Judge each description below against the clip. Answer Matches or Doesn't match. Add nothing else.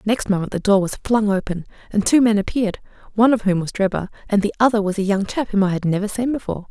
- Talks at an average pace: Doesn't match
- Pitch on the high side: Matches